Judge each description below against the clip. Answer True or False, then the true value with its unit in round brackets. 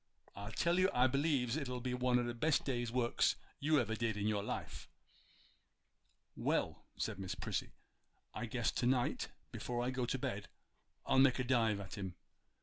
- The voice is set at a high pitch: False (125 Hz)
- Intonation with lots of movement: False (2.7 semitones)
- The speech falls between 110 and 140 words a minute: False (180 wpm)